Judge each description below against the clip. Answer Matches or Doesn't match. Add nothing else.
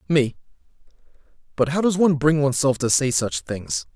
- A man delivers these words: Matches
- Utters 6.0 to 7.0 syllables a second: Doesn't match